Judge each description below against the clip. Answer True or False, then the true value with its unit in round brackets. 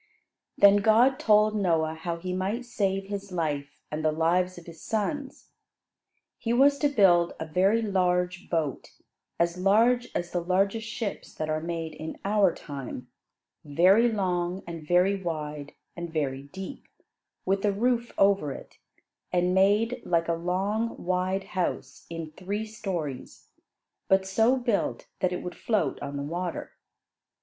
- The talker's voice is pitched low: False (185 Hz)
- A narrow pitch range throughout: False (3.9 semitones)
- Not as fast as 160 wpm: True (150 wpm)